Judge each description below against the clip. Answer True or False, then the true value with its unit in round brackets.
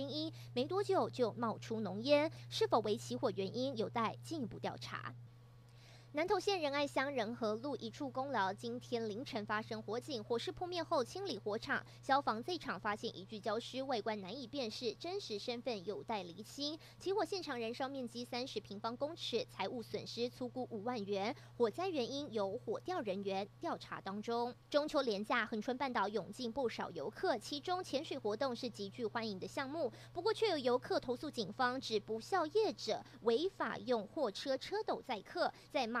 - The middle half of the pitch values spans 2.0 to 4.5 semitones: False (5.2 semitones)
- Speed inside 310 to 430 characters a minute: False (280 characters per minute)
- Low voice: False (245 Hz)